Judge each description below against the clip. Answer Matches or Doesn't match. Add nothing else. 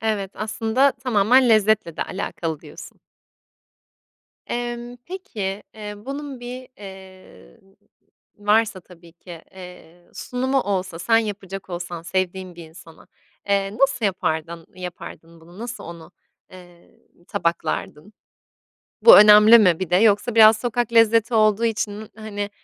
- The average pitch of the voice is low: Doesn't match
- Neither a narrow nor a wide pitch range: Matches